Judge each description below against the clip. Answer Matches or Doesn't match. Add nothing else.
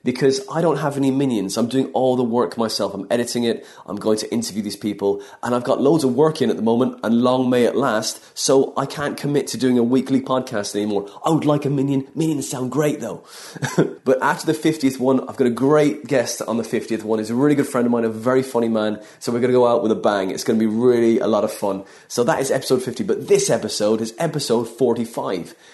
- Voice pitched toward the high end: Doesn't match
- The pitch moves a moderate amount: Matches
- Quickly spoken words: Matches